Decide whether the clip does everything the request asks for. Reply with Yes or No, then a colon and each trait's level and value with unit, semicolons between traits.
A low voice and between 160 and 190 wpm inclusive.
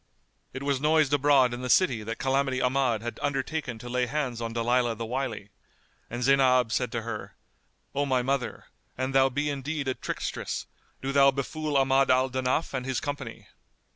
Yes: low, 130 Hz; average, 180 wpm